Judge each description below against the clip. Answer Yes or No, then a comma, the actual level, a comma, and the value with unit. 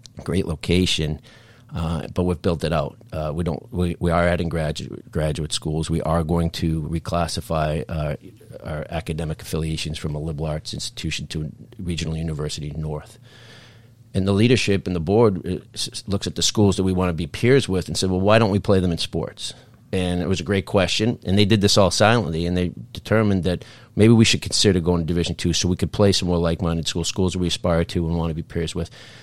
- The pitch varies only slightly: No, average, 3.8 semitones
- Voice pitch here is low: Yes, very low, 90 Hz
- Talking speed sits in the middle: No, fast, 220 wpm